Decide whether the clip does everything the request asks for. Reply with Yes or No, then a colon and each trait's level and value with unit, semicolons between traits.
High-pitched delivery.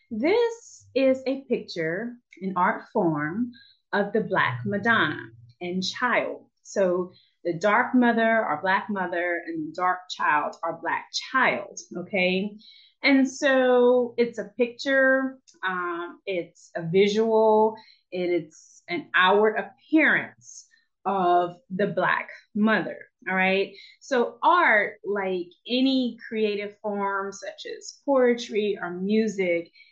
Yes: high, 210 Hz